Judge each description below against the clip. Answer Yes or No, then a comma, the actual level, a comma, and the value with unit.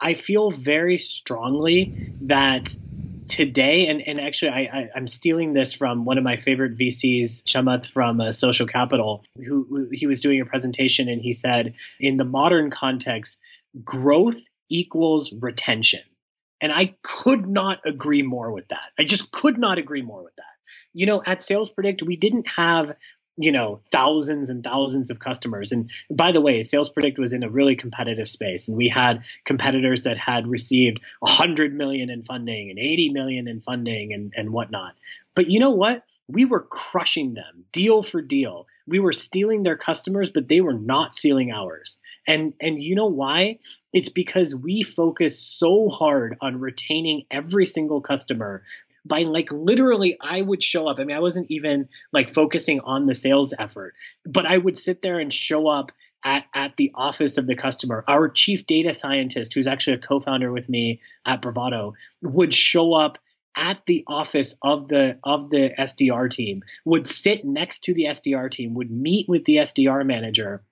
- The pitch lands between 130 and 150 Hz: Yes, medium, 140 Hz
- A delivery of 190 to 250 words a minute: No, average, 180 wpm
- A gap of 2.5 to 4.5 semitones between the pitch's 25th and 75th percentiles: No, average, 5.3 semitones